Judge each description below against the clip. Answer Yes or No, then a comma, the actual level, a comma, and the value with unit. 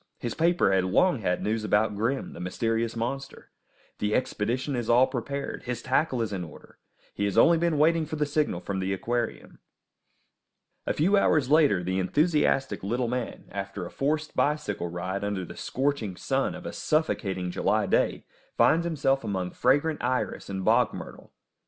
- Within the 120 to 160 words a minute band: No, average, 170 wpm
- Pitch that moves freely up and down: Yes, wide, 6.8 semitones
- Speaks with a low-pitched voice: Yes, low, 120 Hz